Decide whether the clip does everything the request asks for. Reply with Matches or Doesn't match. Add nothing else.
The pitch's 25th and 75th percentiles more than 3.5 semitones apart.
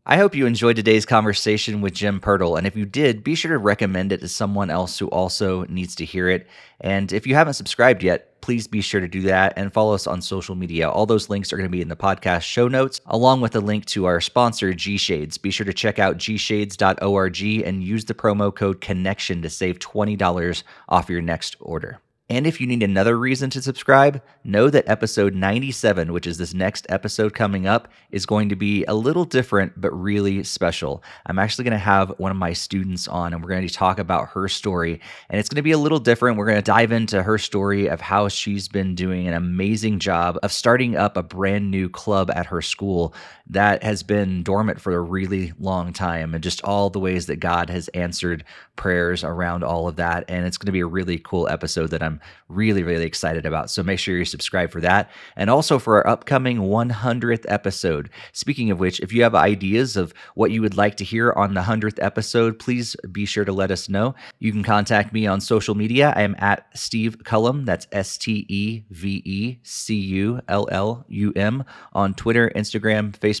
Doesn't match